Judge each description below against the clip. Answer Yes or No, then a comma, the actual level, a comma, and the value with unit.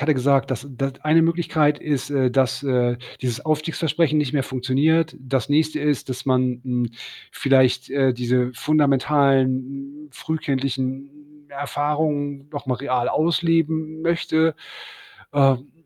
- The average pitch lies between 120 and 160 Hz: Yes, medium, 140 Hz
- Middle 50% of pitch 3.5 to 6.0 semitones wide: No, average, 2.7 semitones